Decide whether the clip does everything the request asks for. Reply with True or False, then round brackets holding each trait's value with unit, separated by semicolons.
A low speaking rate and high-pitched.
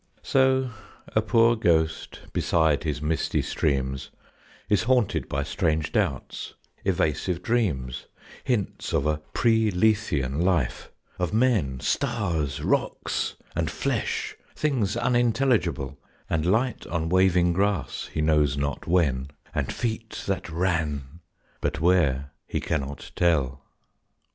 False (115 wpm; 85 Hz)